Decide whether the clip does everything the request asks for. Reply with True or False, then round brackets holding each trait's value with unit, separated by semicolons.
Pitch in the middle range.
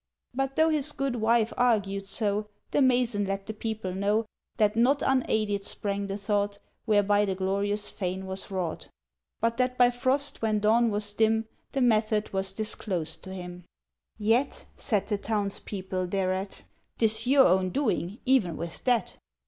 False (210 Hz)